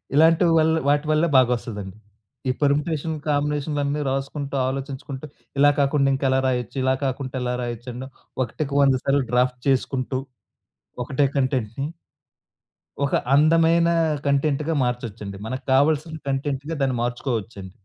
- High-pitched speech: No, low, 135 Hz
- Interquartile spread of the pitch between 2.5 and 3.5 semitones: Yes, average, 2.8 semitones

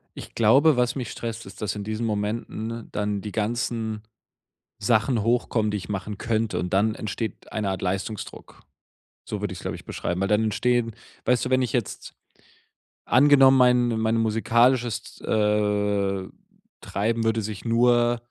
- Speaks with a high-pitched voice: No, low, 110 Hz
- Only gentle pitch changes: Yes, narrow, 2.3 semitones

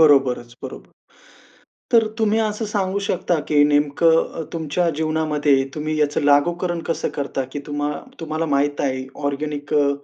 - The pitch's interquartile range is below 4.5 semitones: Yes, average, 2.9 semitones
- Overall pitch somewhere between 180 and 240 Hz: No, medium, 150 Hz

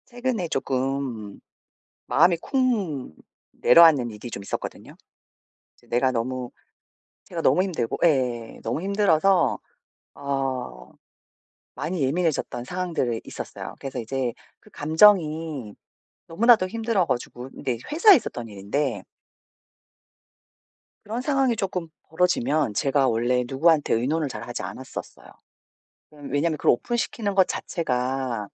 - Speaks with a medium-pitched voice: Yes, medium, 145 Hz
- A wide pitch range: Yes, wide, 6.6 semitones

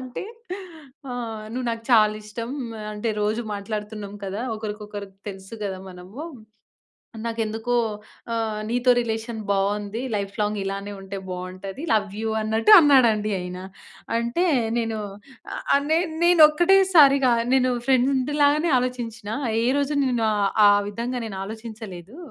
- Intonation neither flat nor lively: Yes, average, 3.5 semitones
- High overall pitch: Yes, high, 225 Hz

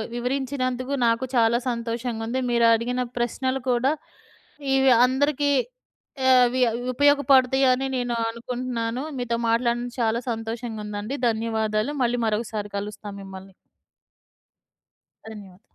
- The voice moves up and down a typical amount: No, narrow, 2.3 semitones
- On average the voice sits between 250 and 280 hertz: No, high, 240 Hz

